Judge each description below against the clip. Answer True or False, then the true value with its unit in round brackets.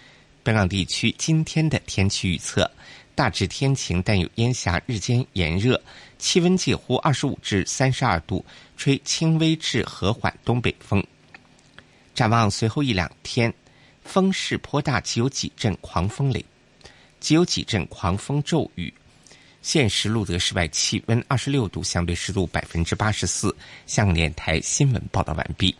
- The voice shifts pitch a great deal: True (7.0 semitones)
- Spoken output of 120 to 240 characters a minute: True (235 characters per minute)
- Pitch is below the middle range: True (115 Hz)